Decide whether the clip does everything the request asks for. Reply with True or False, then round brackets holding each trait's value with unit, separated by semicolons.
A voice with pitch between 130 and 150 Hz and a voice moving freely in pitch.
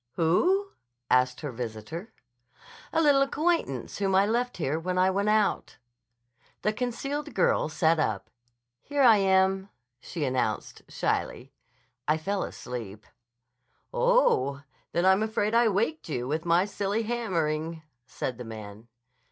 False (190 Hz; 7.9 semitones)